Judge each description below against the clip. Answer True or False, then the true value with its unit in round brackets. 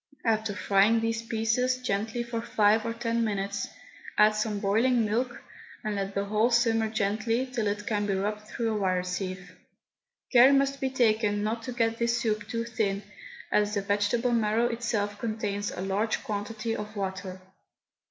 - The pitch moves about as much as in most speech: False (2.2 semitones)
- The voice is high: True (220 Hz)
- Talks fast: False (170 wpm)